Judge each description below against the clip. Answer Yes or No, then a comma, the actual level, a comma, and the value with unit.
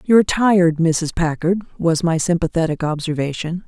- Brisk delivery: No, average, 145 wpm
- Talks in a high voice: No, medium, 170 Hz